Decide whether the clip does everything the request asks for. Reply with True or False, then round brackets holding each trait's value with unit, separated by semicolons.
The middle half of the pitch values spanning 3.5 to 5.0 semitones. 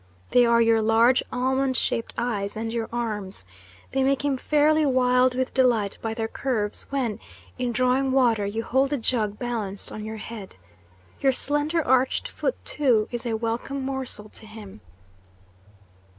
False (3.0 semitones)